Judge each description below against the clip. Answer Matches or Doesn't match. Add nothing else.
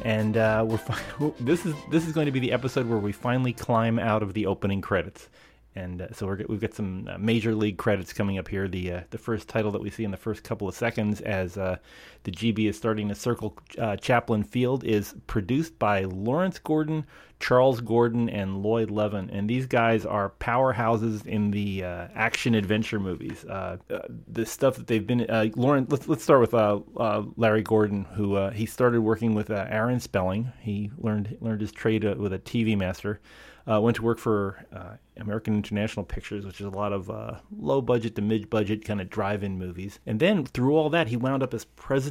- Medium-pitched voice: Doesn't match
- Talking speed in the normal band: Doesn't match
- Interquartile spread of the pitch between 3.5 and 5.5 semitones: Doesn't match